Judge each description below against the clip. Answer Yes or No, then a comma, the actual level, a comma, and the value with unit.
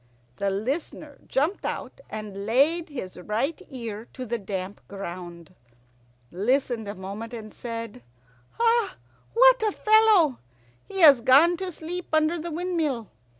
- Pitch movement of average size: No, wide, 8.2 semitones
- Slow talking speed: Yes, slow, 130 wpm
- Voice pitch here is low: No, very high, 260 Hz